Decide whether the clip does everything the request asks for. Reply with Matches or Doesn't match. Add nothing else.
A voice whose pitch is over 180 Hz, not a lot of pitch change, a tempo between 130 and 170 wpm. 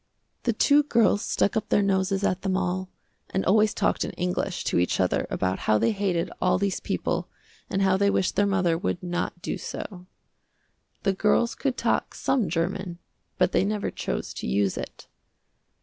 Doesn't match